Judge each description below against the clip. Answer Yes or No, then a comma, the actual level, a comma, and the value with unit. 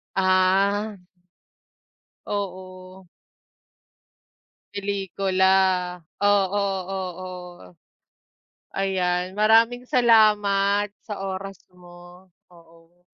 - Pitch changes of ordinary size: No, narrow, 1.9 semitones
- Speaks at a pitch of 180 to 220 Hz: Yes, high, 190 Hz